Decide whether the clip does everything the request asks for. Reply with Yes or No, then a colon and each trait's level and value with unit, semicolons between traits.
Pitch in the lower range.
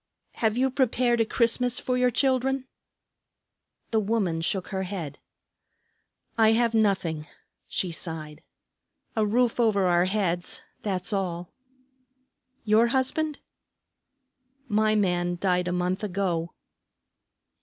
No: high, 205 Hz